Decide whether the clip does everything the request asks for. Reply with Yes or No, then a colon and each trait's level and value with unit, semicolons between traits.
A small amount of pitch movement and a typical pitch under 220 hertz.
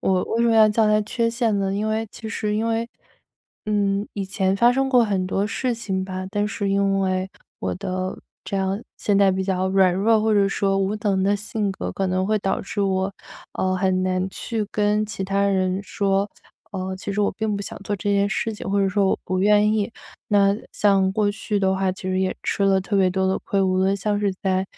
Yes: narrow, 1.8 semitones; high, 200 Hz